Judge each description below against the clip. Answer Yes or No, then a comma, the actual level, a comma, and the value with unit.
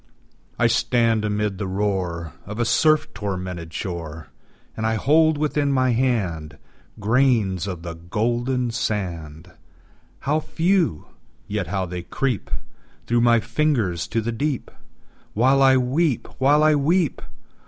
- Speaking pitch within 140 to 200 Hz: No, low, 115 Hz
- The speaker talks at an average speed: No, slow, 130 wpm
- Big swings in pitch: Yes, wide, 6.6 semitones